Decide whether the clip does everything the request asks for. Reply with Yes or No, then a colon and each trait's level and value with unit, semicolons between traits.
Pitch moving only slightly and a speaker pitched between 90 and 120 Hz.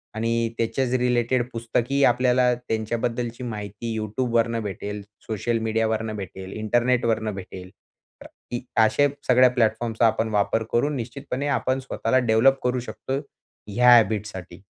Yes: narrow, 2.2 semitones; low, 115 Hz